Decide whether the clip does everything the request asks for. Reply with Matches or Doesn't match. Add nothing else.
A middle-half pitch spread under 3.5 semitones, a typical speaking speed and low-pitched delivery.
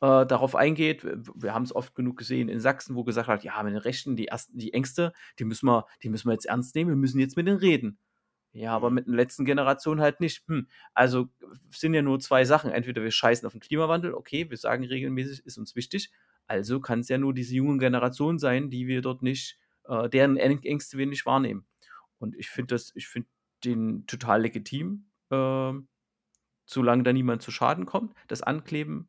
Doesn't match